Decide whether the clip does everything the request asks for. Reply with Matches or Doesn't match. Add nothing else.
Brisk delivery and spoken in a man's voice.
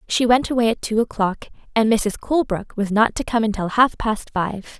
Doesn't match